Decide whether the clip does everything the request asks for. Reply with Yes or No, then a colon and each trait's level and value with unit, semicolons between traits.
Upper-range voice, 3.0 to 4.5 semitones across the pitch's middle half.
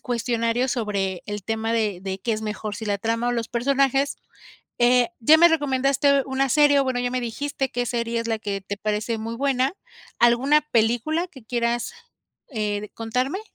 Yes: high, 240 Hz; average, 3.4 semitones